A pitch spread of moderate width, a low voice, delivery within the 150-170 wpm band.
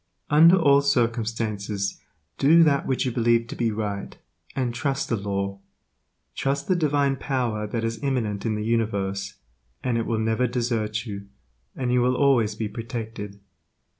Yes: average, 3.9 semitones; low, 115 Hz; average, 160 wpm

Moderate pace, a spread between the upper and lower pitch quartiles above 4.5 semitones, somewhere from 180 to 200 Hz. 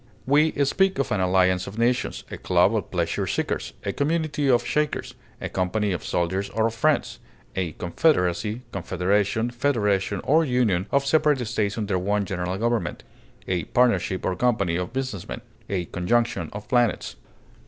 No: average, 160 wpm; average, 5.2 semitones; low, 110 Hz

